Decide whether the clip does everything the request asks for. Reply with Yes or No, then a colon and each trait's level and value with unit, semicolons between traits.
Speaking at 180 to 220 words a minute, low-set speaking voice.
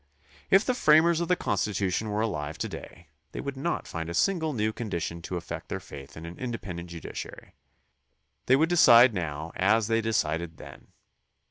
Yes: average, 185 wpm; low, 105 Hz